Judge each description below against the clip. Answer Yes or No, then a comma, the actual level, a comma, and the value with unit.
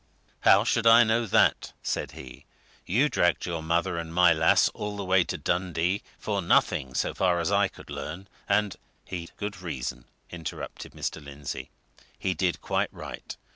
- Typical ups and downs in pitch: Yes, average, 3.5 semitones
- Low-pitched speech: Yes, very low, 90 Hz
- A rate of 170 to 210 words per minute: Yes, average, 175 wpm